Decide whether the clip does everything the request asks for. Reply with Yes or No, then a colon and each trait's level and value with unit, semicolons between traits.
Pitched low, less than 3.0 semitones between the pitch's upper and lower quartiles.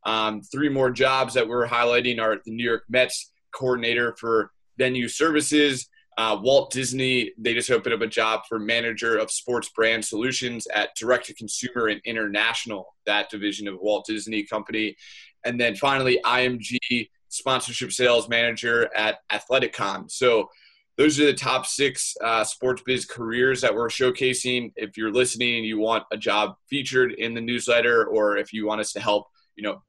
Yes: low, 120 Hz; narrow, 2.5 semitones